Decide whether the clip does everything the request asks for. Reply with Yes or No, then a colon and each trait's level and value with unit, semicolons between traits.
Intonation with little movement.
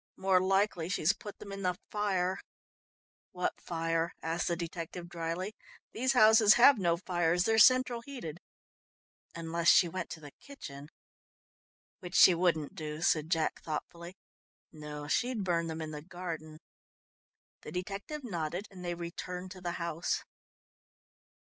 No: average, 3.0 semitones